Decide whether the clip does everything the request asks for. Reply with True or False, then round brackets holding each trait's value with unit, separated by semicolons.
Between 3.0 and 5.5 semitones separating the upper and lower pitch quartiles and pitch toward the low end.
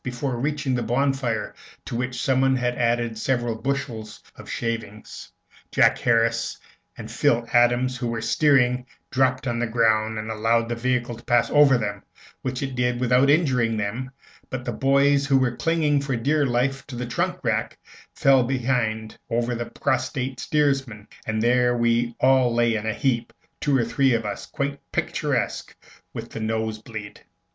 False (2.5 semitones; 120 Hz)